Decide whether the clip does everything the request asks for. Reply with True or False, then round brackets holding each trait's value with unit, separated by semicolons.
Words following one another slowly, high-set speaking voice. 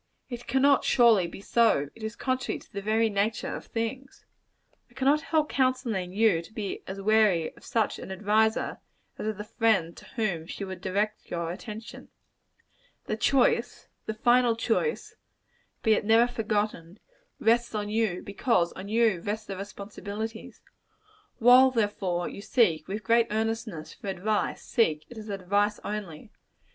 False (155 wpm; 215 Hz)